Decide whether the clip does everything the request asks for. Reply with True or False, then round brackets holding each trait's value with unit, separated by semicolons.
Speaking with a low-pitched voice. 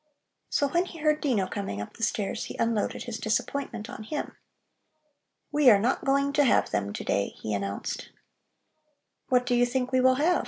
False (245 Hz)